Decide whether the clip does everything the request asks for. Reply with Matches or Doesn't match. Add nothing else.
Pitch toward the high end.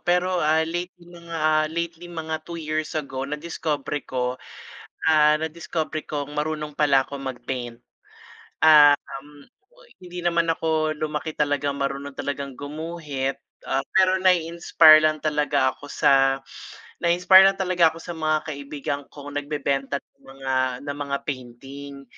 Doesn't match